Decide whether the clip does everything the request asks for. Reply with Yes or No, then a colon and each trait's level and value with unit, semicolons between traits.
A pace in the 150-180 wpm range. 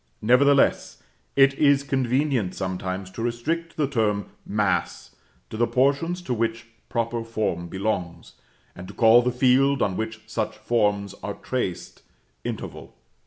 No: slow, 135 wpm